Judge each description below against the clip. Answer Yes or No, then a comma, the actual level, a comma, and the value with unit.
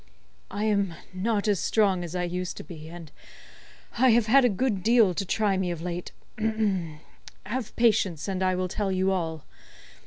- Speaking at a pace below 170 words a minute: No, average, 180 wpm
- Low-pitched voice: No, high, 190 Hz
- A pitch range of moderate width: Yes, average, 3.4 semitones